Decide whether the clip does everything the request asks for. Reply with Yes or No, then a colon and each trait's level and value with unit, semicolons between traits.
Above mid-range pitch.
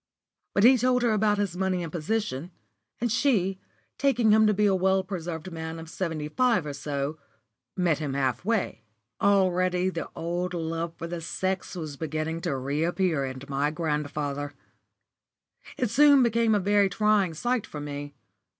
No: medium, 175 Hz